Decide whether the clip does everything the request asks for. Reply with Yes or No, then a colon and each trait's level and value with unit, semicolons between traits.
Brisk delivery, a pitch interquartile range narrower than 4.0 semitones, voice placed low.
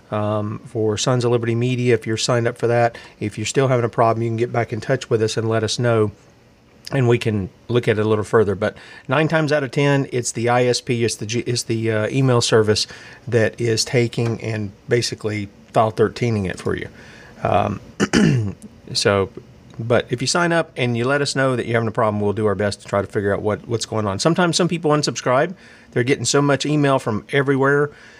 Yes: fast, 230 wpm; average, 2.9 semitones; low, 120 Hz